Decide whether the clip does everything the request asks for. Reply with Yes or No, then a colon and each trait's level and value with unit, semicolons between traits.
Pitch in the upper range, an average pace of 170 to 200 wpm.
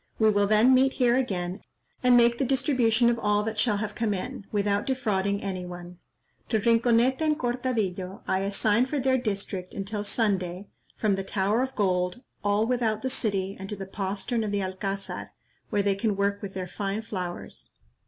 Yes: high, 210 Hz; average, 185 wpm